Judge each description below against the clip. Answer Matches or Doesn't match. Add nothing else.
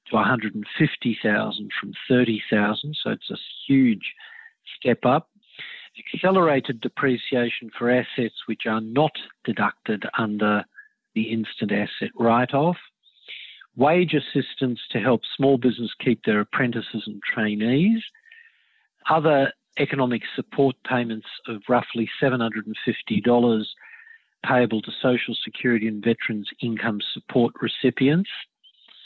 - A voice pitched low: Matches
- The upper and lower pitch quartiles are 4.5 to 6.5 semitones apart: Matches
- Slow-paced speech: Matches